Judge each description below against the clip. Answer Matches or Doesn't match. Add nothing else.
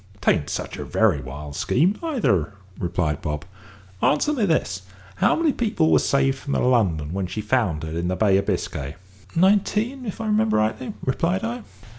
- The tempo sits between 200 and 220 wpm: Doesn't match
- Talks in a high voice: Doesn't match